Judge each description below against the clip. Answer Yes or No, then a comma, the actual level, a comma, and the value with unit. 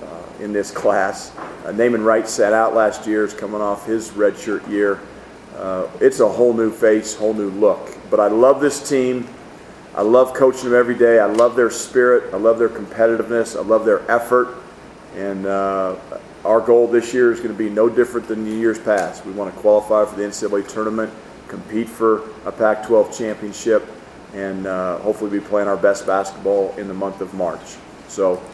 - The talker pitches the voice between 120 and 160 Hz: No, low, 110 Hz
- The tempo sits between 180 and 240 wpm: Yes, average, 195 wpm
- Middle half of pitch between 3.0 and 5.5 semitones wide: No, narrow, 2.6 semitones